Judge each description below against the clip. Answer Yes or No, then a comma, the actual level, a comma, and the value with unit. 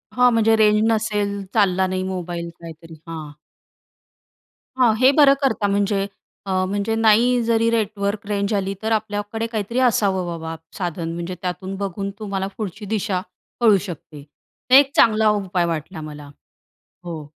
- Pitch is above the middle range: Yes, high, 200 Hz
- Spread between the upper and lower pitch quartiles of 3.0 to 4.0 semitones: Yes, average, 3.5 semitones